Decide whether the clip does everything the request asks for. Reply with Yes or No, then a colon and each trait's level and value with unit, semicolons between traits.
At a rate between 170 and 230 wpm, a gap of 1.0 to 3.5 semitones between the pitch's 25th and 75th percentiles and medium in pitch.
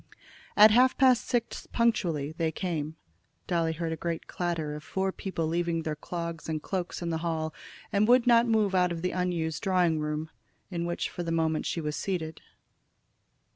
Yes: average, 180 wpm; average, 3.0 semitones; medium, 170 Hz